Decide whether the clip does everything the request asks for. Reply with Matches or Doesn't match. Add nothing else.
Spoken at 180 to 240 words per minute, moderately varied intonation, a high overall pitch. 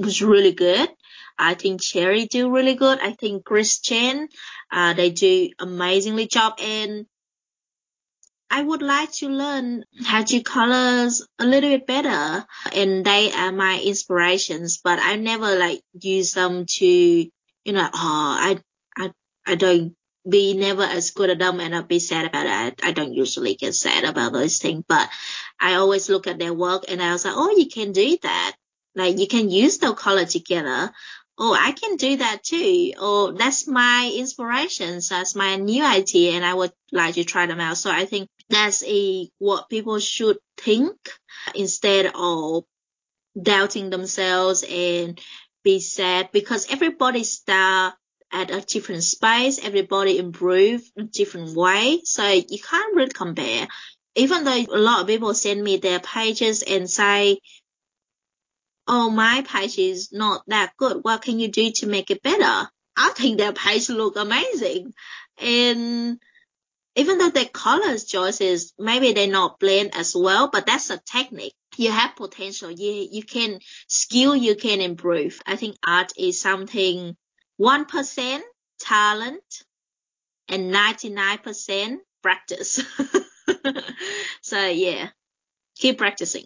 Doesn't match